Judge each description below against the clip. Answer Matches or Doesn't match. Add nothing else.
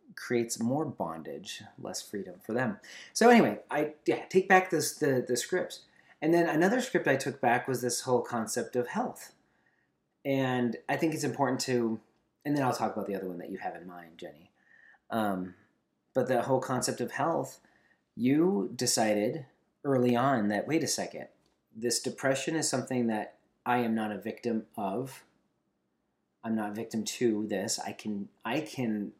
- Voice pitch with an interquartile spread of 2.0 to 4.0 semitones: Doesn't match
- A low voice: Matches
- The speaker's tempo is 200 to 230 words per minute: Doesn't match